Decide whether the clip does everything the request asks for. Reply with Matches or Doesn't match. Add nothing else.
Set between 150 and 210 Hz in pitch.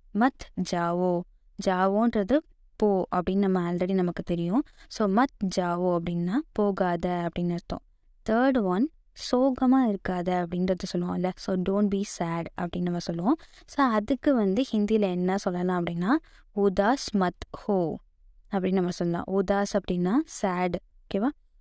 Matches